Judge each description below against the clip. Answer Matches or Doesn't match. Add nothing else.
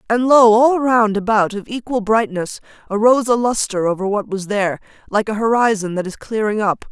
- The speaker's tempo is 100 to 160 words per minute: Doesn't match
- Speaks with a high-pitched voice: Matches